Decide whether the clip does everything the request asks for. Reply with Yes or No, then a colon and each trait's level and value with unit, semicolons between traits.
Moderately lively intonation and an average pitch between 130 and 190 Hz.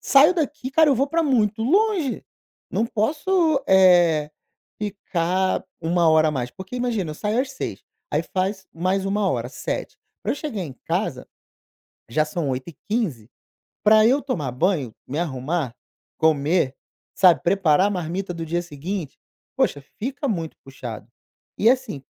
No: wide, 7.2 semitones; medium, 185 Hz